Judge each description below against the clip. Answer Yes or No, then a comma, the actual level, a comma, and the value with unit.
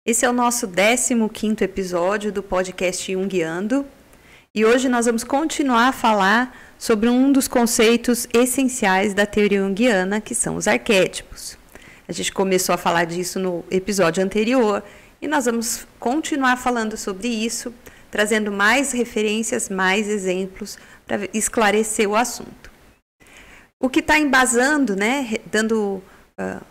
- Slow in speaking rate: No, average, 135 wpm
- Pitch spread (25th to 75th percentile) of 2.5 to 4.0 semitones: Yes, average, 3.7 semitones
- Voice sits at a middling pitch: No, high, 220 Hz